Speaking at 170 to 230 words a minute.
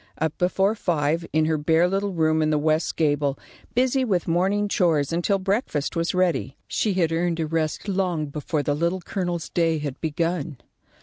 Yes: average, 180 wpm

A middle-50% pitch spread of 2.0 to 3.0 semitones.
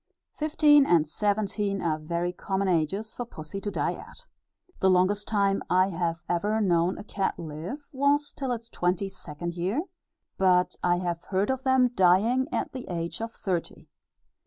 No: average, 4.6 semitones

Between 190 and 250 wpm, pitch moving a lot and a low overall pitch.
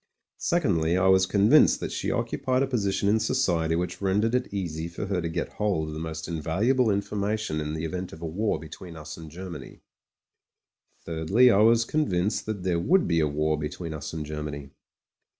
No: average, 195 wpm; average, 4.8 semitones; very low, 90 Hz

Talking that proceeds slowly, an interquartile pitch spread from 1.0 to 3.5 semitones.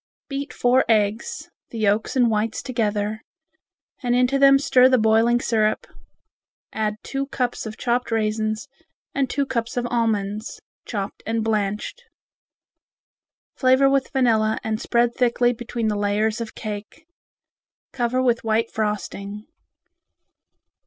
Yes: slow, 125 wpm; narrow, 2.6 semitones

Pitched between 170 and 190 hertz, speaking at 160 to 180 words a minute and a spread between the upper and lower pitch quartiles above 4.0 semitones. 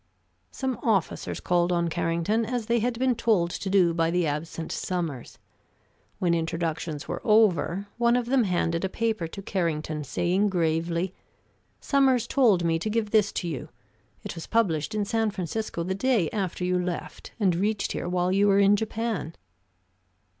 Yes: medium, 185 Hz; average, 170 wpm; average, 4.7 semitones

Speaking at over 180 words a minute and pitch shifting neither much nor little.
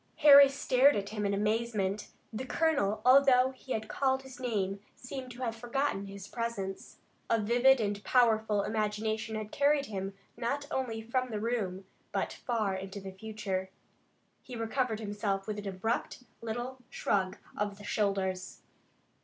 No: average, 155 wpm; average, 4.0 semitones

